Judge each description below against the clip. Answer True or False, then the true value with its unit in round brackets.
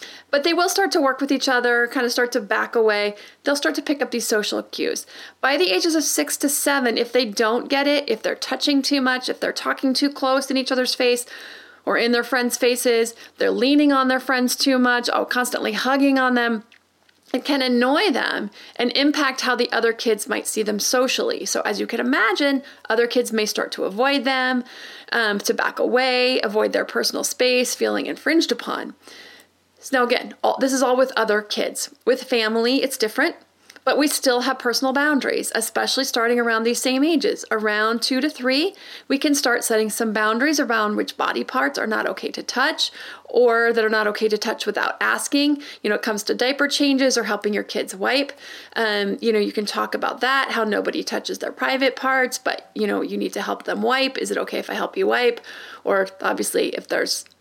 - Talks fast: True (215 wpm)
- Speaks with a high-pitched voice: True (255 Hz)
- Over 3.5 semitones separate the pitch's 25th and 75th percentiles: False (3.2 semitones)